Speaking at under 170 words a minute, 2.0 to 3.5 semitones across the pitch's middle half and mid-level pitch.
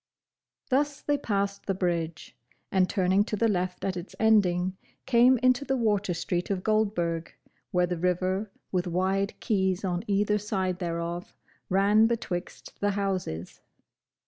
No: average, 145 wpm; average, 2.9 semitones; high, 195 Hz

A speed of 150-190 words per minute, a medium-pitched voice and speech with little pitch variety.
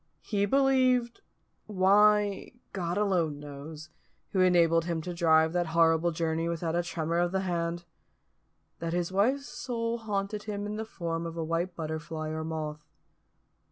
No: average, 155 wpm; medium, 175 Hz; average, 3.8 semitones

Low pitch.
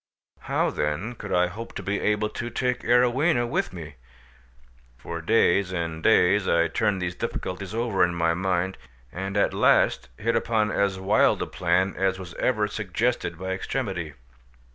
Yes: very low, 95 Hz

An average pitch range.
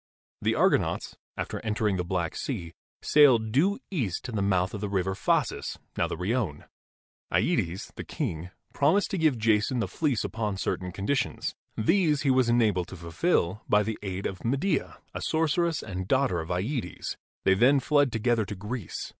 No: wide, 6.5 semitones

